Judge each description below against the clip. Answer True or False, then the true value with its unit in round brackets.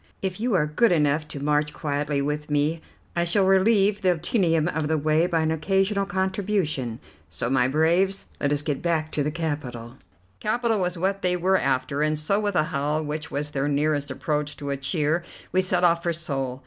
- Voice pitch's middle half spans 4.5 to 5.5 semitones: False (3.8 semitones)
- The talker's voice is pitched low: False (155 Hz)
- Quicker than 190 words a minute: True (200 wpm)